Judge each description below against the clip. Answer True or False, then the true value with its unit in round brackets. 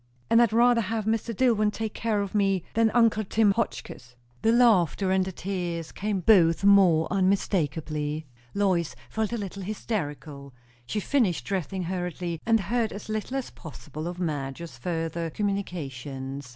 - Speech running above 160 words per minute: False (150 wpm)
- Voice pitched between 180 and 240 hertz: True (190 Hz)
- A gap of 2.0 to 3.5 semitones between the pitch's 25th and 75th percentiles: False (4.9 semitones)